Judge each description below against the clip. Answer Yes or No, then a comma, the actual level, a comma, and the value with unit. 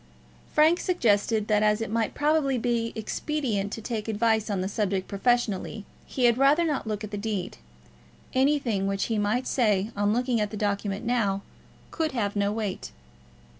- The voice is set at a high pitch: Yes, high, 220 Hz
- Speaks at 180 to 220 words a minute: No, average, 170 wpm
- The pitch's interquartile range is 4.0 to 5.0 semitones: No, average, 3.3 semitones